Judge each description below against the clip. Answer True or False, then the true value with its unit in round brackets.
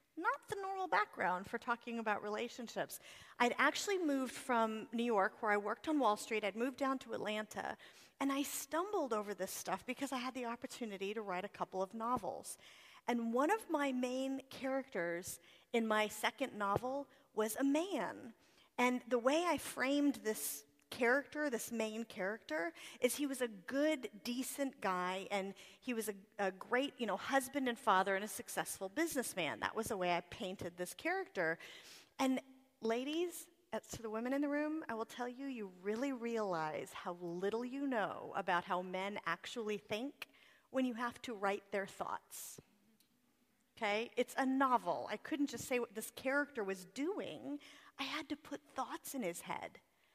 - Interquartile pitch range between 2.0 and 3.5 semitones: False (4.8 semitones)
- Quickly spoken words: False (175 wpm)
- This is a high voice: True (240 Hz)